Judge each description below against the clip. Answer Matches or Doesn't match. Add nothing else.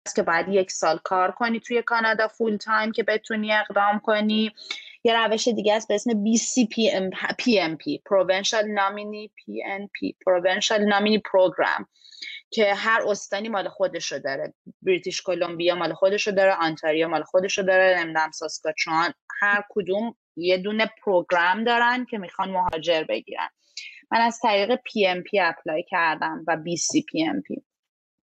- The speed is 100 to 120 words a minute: Doesn't match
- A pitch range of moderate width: Matches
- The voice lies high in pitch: Matches